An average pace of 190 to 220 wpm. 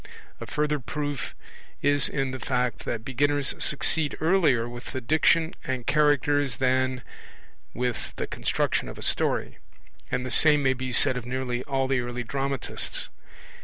No: average, 155 wpm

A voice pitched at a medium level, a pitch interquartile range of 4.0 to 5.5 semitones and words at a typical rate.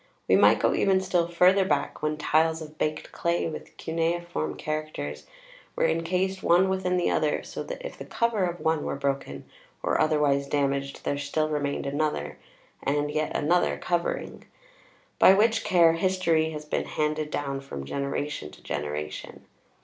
No: medium, 155 Hz; average, 3.4 semitones; average, 160 wpm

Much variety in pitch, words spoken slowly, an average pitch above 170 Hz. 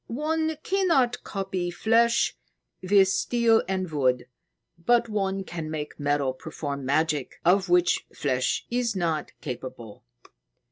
Yes: wide, 7.9 semitones; slow, 120 wpm; medium, 185 Hz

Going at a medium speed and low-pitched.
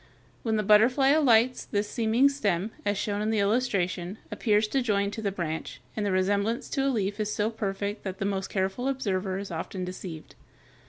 No: average, 195 wpm; high, 205 Hz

